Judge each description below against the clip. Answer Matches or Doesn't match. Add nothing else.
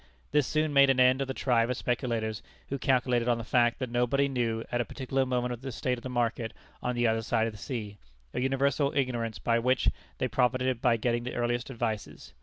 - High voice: Doesn't match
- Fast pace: Matches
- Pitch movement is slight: Matches